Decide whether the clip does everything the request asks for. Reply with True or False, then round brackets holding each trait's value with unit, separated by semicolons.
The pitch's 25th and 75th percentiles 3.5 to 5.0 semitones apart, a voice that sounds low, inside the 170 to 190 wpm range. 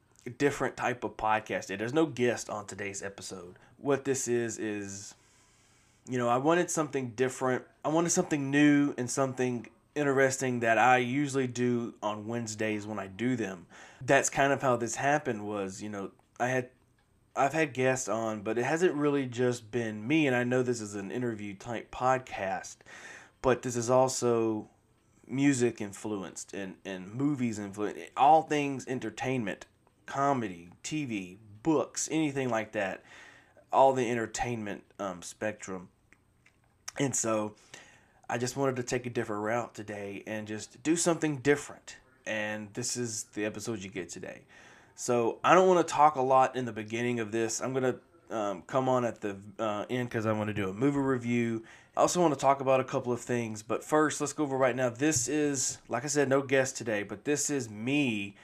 True (3.9 semitones; 120 Hz; 180 wpm)